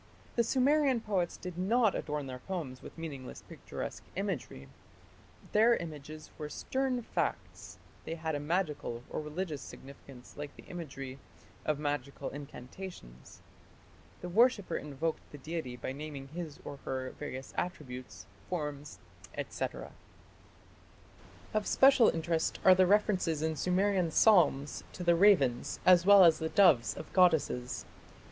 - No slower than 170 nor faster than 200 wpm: No, slow, 135 wpm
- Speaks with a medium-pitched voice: Yes, medium, 160 Hz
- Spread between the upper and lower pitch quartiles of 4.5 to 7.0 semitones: Yes, average, 5.1 semitones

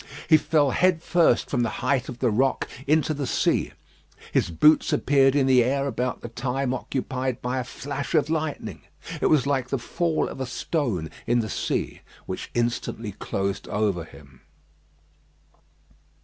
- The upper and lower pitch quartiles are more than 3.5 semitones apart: No, average, 3.2 semitones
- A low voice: Yes, low, 130 Hz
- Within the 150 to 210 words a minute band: Yes, average, 165 wpm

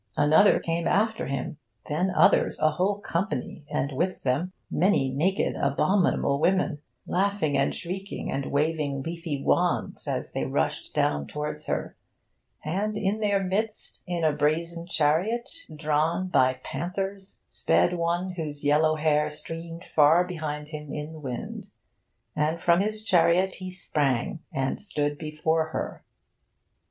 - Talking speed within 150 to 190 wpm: No, average, 140 wpm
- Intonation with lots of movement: No, average, 3.9 semitones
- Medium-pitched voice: Yes, medium, 165 Hz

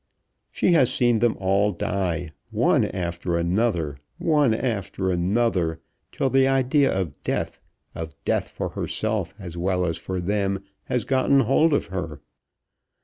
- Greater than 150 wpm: No, average, 145 wpm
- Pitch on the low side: Yes, very low, 95 Hz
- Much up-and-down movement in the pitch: Yes, wide, 6.1 semitones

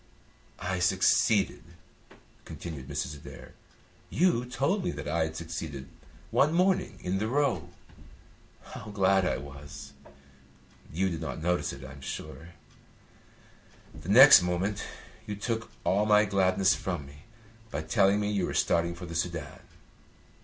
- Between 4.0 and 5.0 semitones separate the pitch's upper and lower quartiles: Yes, average, 4.5 semitones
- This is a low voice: Yes, very low, 95 Hz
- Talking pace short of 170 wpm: Yes, average, 140 wpm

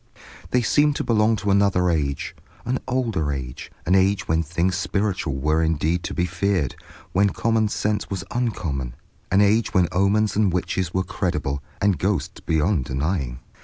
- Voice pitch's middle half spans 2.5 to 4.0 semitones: No, average, 4.8 semitones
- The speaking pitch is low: Yes, very low, 90 Hz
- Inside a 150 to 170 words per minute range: Yes, average, 165 wpm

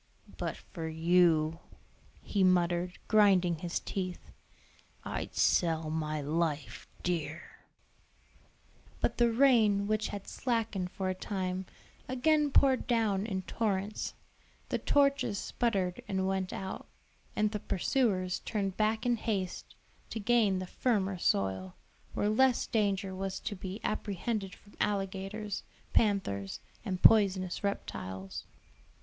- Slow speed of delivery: Yes, slow, 120 wpm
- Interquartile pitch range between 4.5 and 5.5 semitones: No, average, 3.2 semitones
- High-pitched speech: Yes, high, 195 Hz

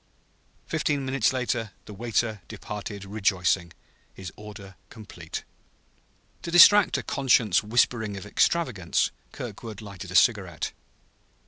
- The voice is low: Yes, low, 105 Hz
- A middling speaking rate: No, slow, 110 wpm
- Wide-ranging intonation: No, average, 4.0 semitones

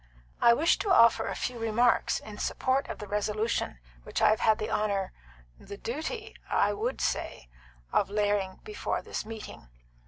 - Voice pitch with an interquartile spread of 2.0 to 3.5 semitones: Yes, average, 2.9 semitones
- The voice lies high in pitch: Yes, high, 215 Hz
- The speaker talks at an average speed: Yes, average, 165 wpm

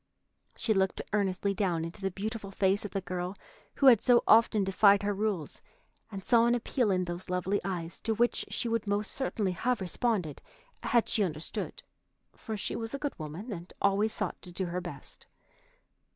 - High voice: Yes, high, 200 Hz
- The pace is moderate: Yes, average, 185 wpm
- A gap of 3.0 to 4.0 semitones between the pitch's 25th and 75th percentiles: Yes, average, 3.4 semitones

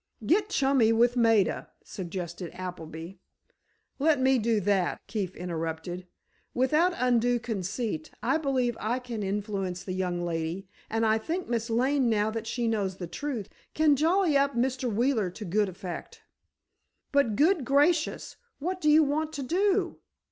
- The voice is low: No, high, 230 Hz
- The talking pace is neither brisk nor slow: Yes, average, 150 wpm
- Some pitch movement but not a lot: No, wide, 6.7 semitones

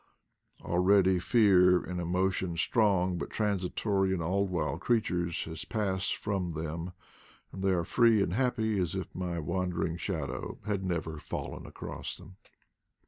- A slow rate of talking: No, average, 145 wpm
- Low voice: Yes, very low, 90 Hz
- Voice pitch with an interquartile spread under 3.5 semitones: Yes, narrow, 2.4 semitones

